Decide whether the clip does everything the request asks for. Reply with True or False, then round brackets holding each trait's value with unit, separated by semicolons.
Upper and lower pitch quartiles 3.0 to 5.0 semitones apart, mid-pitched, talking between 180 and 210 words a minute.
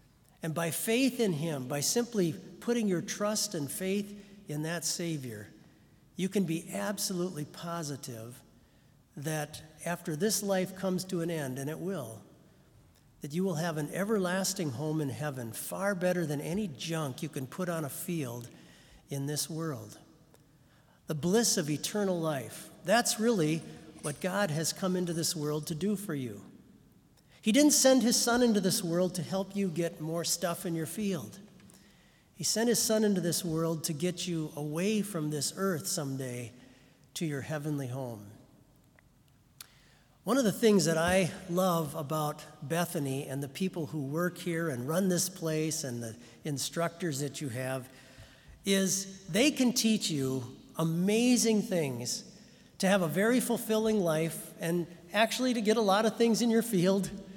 False (4.7 semitones; 170 Hz; 165 wpm)